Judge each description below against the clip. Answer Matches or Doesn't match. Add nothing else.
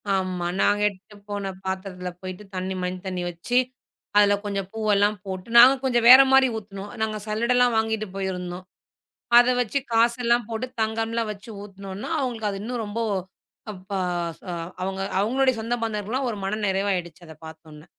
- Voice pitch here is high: Matches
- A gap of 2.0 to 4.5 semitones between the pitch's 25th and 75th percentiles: Matches